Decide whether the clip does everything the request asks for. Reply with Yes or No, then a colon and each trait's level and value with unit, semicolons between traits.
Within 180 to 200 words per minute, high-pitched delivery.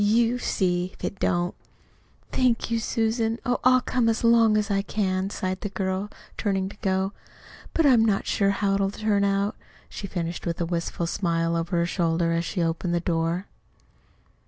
Yes: average, 185 wpm; high, 195 Hz